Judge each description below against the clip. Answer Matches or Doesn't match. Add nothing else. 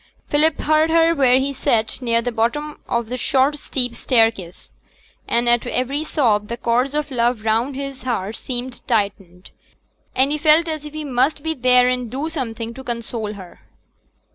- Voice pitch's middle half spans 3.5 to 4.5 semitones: Matches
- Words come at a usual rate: Matches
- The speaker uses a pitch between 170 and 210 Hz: Doesn't match